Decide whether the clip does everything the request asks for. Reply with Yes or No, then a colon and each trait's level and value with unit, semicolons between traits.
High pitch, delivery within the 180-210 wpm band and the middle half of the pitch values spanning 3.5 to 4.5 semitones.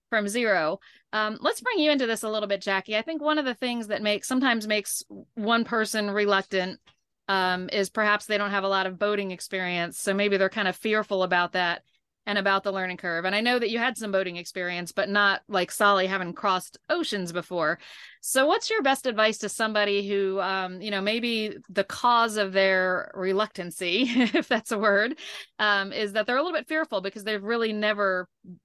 No: high, 205 Hz; fast, 205 wpm; average, 2.9 semitones